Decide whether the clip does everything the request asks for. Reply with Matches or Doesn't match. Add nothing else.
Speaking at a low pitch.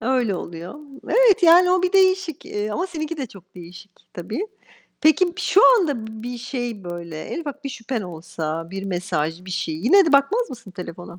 Doesn't match